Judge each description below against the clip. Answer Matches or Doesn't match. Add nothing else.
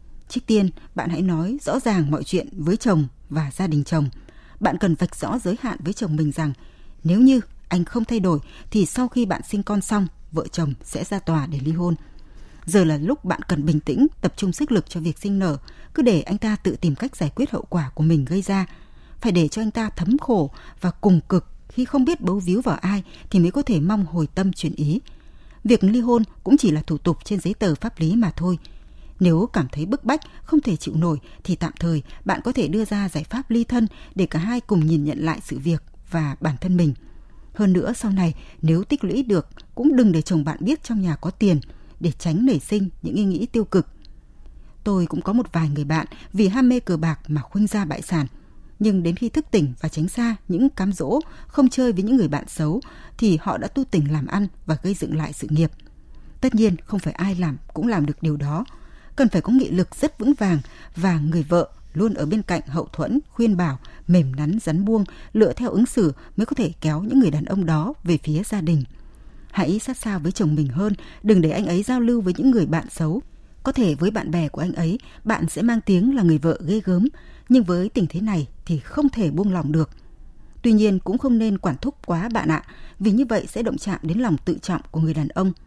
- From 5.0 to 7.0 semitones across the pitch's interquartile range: Matches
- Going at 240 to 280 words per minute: Matches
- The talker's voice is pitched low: Doesn't match